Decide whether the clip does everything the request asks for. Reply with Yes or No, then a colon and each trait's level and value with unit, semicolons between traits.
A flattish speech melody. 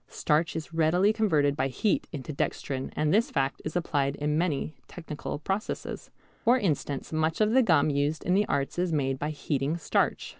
No: average, 3.9 semitones